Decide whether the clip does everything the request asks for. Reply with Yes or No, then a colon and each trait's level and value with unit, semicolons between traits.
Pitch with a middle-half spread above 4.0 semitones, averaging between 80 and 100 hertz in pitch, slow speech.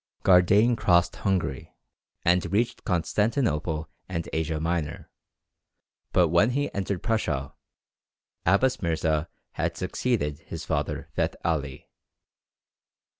Yes: average, 4.5 semitones; very low, 85 Hz; slow, 100 wpm